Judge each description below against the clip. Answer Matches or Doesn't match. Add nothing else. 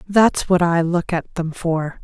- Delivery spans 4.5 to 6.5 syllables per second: Doesn't match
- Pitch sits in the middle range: Matches